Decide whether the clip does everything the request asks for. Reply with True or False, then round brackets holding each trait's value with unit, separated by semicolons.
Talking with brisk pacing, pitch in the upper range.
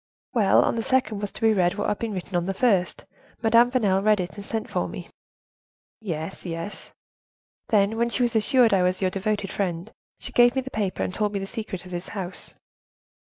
True (215 wpm; 205 Hz)